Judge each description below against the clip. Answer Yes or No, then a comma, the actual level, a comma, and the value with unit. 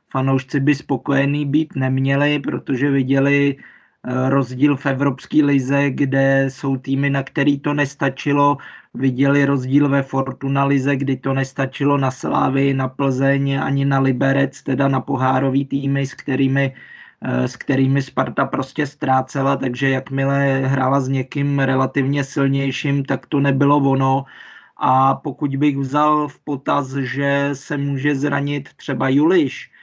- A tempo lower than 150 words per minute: Yes, average, 135 wpm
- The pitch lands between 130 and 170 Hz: Yes, medium, 140 Hz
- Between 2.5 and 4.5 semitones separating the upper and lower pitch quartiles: No, narrow, 1.0 semitones